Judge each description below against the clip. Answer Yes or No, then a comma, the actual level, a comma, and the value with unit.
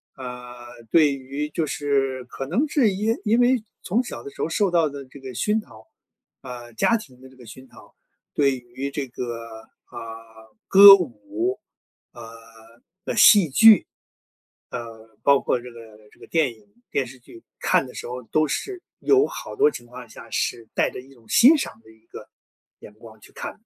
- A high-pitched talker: No, low, 130 Hz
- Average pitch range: No, wide, 6.3 semitones